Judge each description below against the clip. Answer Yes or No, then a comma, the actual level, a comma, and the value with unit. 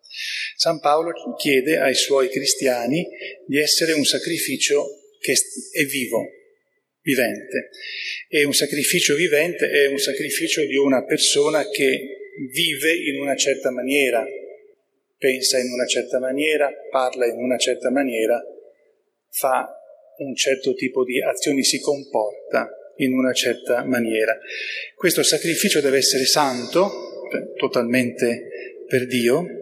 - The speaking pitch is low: No, medium, 150 Hz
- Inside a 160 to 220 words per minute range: No, average, 120 wpm